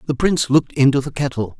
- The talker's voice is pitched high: No, medium, 140 Hz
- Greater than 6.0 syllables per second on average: Yes, 7.0 syllables/s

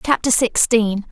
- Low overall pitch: No, high, 230 Hz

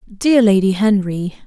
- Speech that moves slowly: Yes, slow, 125 wpm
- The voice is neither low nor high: No, high, 205 Hz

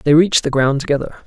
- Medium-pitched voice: Yes, medium, 150 Hz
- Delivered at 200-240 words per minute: Yes, fast, 235 wpm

